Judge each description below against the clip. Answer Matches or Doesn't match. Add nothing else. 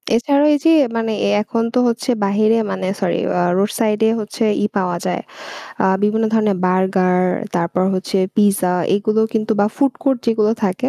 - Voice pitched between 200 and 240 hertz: Matches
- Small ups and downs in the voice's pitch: Doesn't match